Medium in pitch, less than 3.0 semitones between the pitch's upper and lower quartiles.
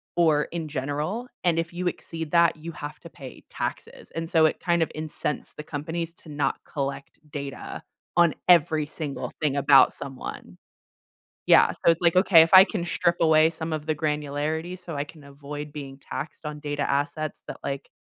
Yes: medium, 155 Hz; narrow, 2.5 semitones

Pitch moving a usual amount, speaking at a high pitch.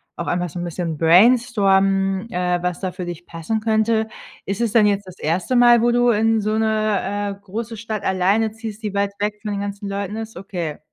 Yes: average, 3.2 semitones; high, 205 Hz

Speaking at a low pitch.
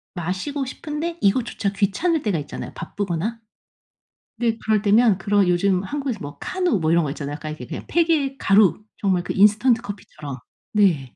No: high, 205 Hz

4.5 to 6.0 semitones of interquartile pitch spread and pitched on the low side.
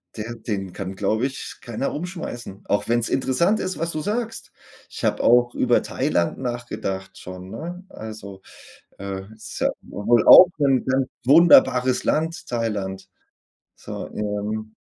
Yes: average, 5.2 semitones; low, 120 Hz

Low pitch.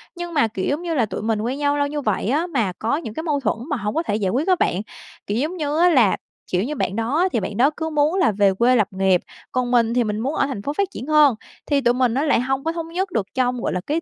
No: very high, 260 Hz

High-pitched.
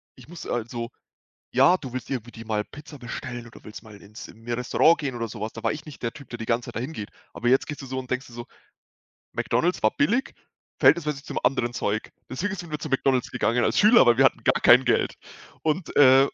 No: low, 125 Hz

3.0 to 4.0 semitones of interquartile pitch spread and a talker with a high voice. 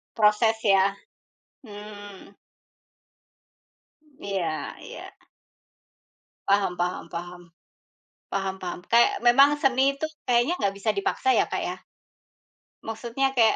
Yes: average, 3.6 semitones; high, 210 Hz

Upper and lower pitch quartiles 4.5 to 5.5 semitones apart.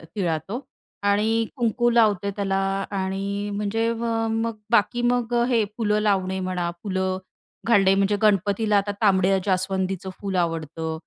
No: narrow, 2.4 semitones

